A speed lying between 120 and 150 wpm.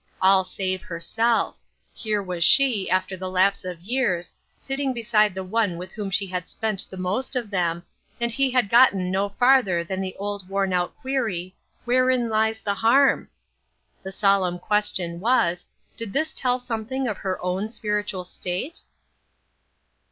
No: average, 160 wpm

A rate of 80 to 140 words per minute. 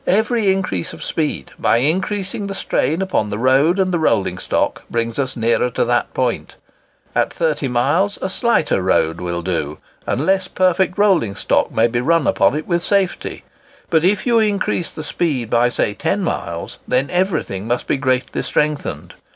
No: average, 175 wpm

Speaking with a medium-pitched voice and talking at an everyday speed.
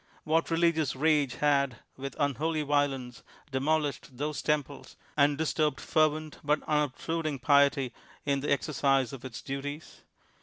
No: medium, 145 Hz; slow, 125 wpm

